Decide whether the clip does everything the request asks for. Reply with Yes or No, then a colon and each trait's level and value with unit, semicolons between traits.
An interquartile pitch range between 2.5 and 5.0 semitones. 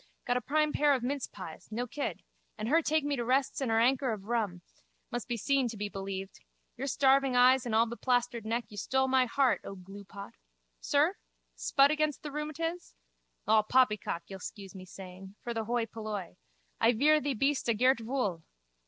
Yes: average, 4.7 semitones